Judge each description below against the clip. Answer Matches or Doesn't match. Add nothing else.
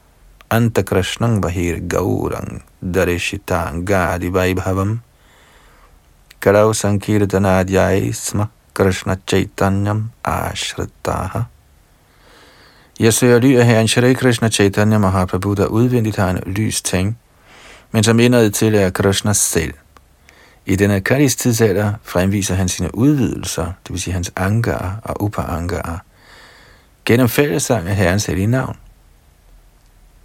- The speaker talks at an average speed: Doesn't match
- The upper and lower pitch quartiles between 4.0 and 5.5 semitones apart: Doesn't match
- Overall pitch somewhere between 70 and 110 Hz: Matches